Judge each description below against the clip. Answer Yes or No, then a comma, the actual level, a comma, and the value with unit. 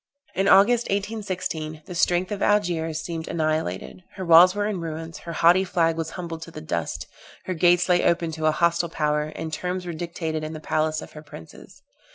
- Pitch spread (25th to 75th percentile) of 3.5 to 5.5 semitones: No, narrow, 2.4 semitones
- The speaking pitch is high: No, medium, 165 Hz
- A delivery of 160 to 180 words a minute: No, average, 200 wpm